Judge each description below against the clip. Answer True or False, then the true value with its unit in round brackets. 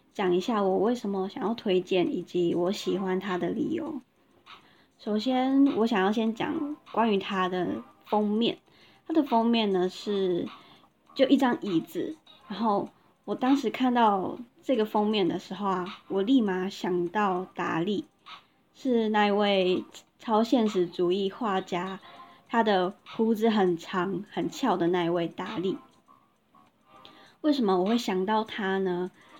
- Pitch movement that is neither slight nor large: True (3.9 semitones)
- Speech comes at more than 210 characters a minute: False (205 characters per minute)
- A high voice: True (200 Hz)